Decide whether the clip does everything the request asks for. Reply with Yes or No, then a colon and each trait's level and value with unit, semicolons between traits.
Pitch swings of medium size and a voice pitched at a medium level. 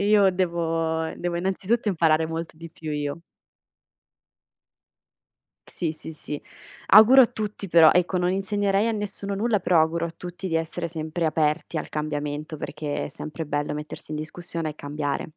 Yes: average, 3.5 semitones; medium, 165 Hz